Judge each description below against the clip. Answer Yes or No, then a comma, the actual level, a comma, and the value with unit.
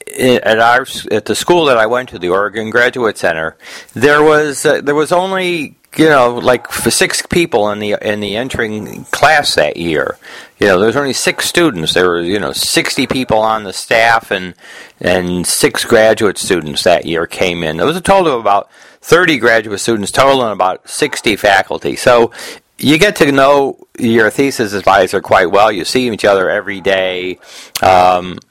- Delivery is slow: No, average, 185 wpm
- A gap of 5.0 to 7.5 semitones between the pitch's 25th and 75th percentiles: Yes, wide, 5.5 semitones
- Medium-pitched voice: No, low, 115 Hz